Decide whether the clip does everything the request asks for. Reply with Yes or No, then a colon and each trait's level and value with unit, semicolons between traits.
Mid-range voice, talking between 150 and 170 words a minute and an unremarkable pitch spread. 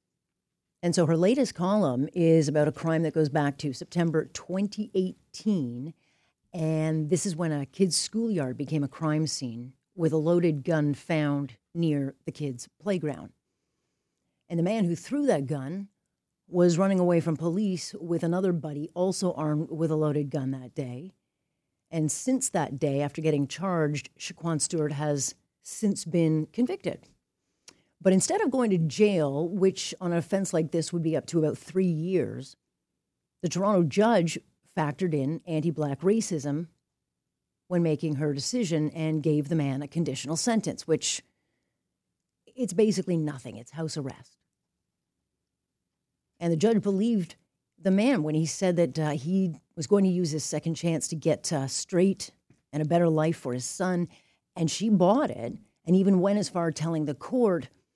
Yes: medium, 165 Hz; average, 165 wpm; average, 3.5 semitones